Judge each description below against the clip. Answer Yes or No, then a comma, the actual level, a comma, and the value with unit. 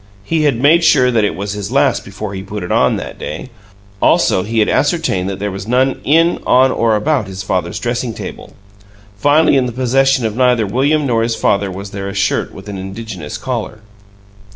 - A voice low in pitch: Yes, low, 115 Hz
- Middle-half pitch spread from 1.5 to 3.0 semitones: No, average, 5.0 semitones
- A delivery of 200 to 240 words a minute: Yes, fast, 205 wpm